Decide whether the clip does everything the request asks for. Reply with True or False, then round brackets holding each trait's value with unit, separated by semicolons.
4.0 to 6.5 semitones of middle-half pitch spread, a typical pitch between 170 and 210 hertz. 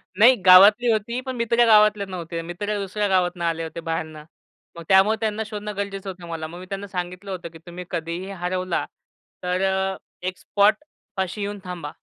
False (3.0 semitones; 190 Hz)